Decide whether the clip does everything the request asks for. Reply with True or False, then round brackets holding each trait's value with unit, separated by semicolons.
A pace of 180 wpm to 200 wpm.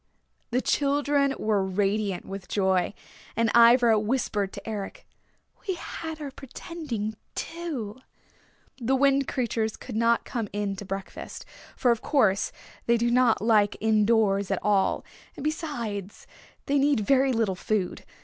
False (140 wpm)